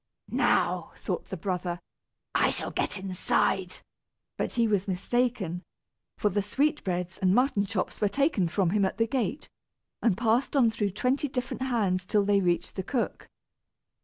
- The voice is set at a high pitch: Yes, high, 205 Hz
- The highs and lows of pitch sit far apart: No, average, 4.7 semitones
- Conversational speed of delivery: Yes, average, 160 wpm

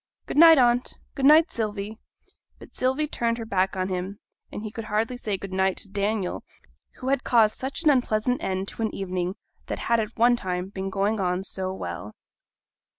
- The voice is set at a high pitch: Yes, high, 210 Hz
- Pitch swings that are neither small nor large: Yes, average, 4.1 semitones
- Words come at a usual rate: Yes, average, 195 wpm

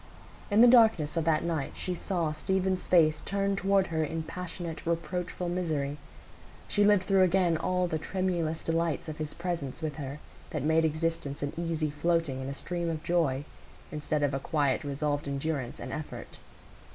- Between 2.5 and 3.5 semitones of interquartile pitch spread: Yes, average, 3.1 semitones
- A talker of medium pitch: Yes, medium, 165 Hz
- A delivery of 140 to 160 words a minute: No, average, 175 wpm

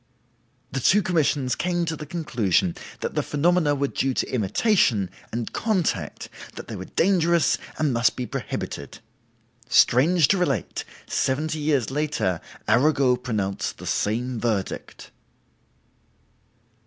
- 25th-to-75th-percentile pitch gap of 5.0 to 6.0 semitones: Yes, wide, 5.4 semitones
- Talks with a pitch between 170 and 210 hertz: No, medium, 140 Hz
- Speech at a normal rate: No, slow, 125 wpm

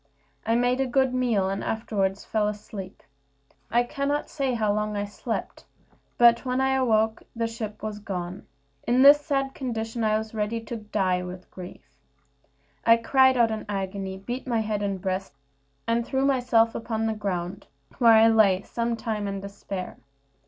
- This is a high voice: Yes, high, 220 Hz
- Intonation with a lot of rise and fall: No, average, 3.3 semitones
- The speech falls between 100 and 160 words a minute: No, average, 170 wpm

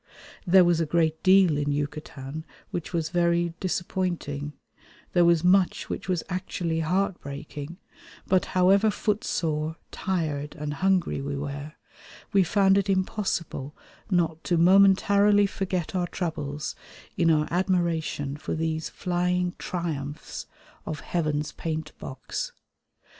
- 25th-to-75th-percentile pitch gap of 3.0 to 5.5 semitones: Yes, average, 3.4 semitones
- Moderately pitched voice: Yes, medium, 170 Hz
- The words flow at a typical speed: No, slow, 120 wpm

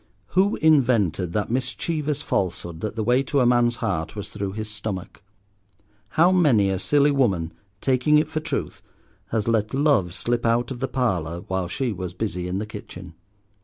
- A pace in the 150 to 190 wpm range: Yes, average, 175 wpm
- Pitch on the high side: No, low, 115 Hz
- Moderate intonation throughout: No, wide, 6.2 semitones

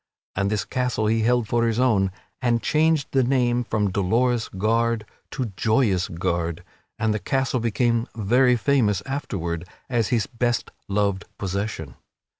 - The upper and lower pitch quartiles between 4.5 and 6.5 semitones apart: No, average, 3.7 semitones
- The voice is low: Yes, low, 115 Hz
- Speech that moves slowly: No, average, 145 wpm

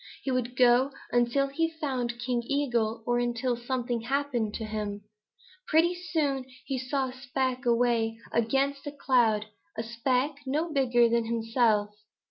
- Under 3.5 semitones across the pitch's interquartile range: Yes, average, 2.8 semitones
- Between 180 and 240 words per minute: No, average, 150 wpm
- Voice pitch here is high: Yes, high, 245 Hz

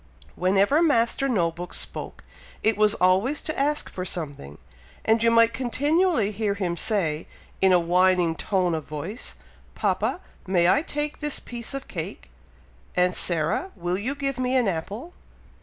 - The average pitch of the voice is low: No, high, 205 Hz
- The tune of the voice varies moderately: No, wide, 6.5 semitones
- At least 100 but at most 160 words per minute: Yes, average, 155 wpm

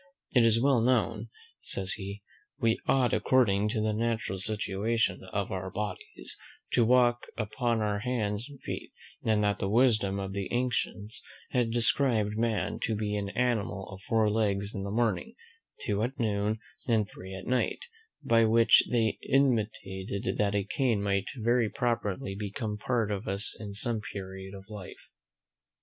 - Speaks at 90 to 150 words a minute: No, average, 160 wpm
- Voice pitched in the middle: No, low, 110 Hz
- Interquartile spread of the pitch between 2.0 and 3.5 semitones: Yes, average, 2.7 semitones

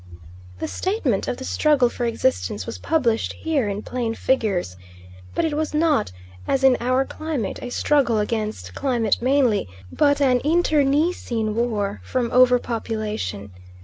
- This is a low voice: No, high, 245 Hz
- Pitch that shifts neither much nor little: Yes, average, 4.8 semitones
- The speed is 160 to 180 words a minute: No, average, 145 wpm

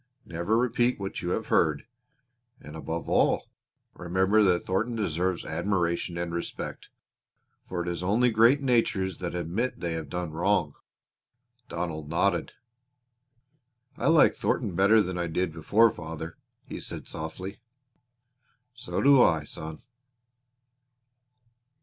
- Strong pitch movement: No, average, 4.3 semitones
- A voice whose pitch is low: Yes, very low, 90 Hz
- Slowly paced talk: Yes, slow, 130 wpm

